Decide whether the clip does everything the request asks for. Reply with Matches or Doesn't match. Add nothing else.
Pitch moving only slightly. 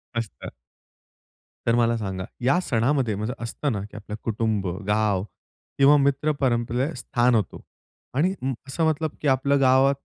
Doesn't match